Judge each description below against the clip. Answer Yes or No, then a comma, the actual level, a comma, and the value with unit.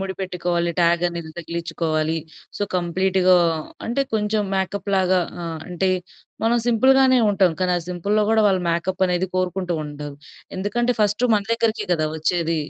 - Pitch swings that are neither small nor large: Yes, average, 3.2 semitones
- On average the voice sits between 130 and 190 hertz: Yes, medium, 185 Hz